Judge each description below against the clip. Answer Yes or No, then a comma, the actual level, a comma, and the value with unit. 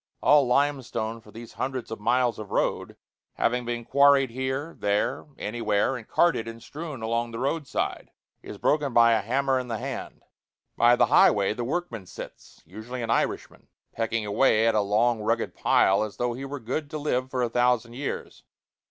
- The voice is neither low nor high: No, low, 120 Hz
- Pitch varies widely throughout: No, average, 3.0 semitones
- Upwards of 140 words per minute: Yes, average, 185 wpm